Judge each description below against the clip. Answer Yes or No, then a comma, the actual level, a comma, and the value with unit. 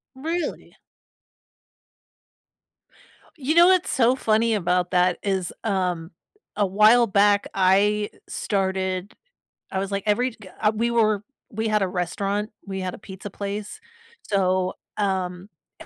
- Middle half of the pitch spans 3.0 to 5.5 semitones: No, narrow, 2.5 semitones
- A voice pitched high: Yes, high, 200 Hz